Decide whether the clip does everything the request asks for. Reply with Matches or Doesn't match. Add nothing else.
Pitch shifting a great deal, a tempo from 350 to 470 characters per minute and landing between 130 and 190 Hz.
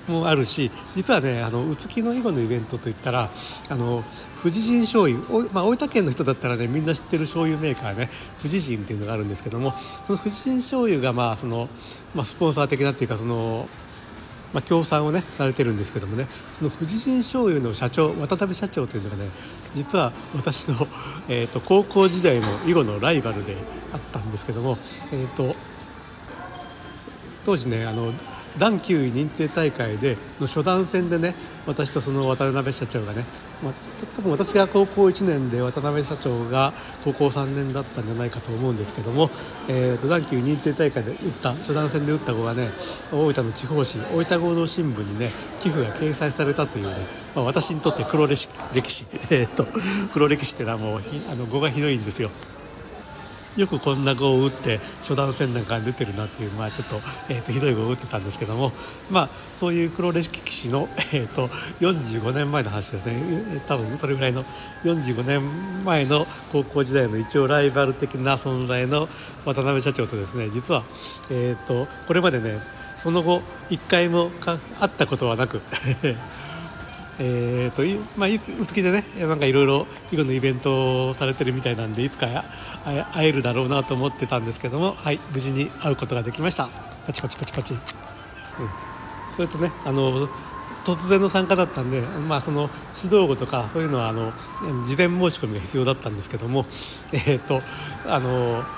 Doesn't match